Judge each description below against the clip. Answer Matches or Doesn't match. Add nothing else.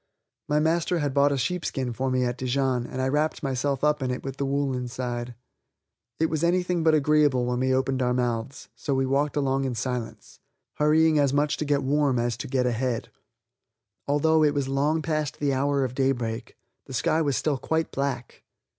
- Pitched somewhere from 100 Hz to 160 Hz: Matches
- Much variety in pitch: Doesn't match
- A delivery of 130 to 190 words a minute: Doesn't match